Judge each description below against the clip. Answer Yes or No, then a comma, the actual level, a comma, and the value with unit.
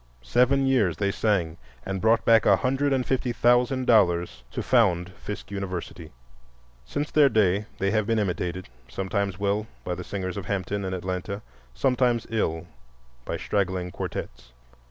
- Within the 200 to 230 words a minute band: No, average, 150 wpm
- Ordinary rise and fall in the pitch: Yes, average, 4.2 semitones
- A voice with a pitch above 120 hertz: No, low, 100 Hz